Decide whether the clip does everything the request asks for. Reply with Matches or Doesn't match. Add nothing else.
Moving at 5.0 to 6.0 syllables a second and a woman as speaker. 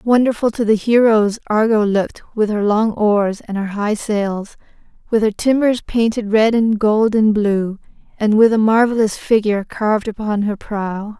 Doesn't match